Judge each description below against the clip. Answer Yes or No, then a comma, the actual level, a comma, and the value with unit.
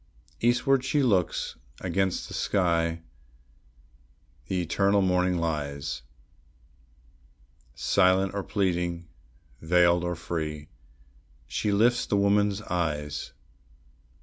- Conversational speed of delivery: No, slow, 90 wpm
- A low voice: Yes, very low, 90 Hz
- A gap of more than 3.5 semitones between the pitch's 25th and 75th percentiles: No, average, 3.1 semitones